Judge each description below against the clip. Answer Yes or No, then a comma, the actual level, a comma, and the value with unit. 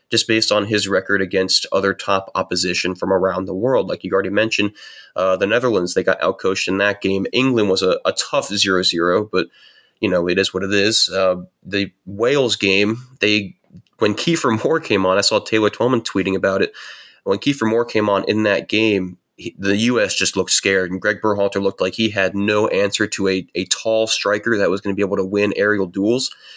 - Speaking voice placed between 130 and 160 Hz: No, low, 100 Hz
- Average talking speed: No, fast, 210 wpm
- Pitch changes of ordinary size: No, narrow, 2.2 semitones